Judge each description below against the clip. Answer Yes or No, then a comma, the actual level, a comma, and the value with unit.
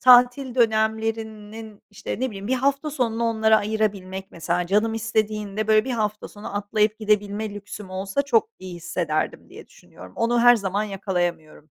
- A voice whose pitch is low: No, high, 215 Hz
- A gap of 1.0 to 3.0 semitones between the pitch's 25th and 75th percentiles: Yes, narrow, 2.4 semitones